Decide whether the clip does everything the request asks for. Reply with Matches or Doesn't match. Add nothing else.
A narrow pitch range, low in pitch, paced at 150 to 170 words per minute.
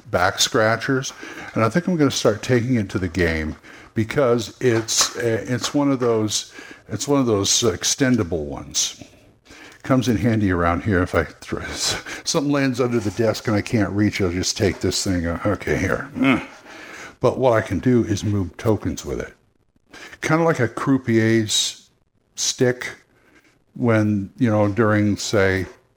Doesn't match